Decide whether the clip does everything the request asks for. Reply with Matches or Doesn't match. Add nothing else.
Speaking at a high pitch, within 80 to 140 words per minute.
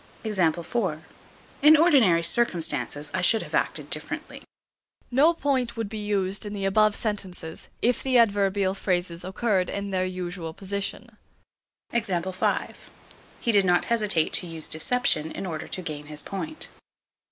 Matches